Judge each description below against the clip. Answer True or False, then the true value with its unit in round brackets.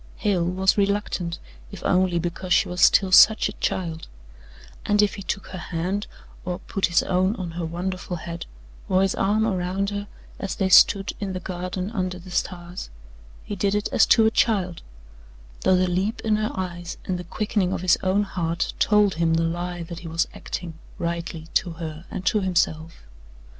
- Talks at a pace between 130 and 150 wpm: False (190 wpm)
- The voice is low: False (185 Hz)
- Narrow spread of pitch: True (2.3 semitones)